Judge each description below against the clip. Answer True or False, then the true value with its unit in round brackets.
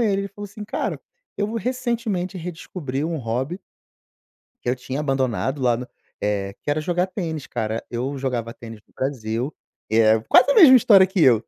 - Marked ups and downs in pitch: True (8.4 semitones)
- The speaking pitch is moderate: True (145 Hz)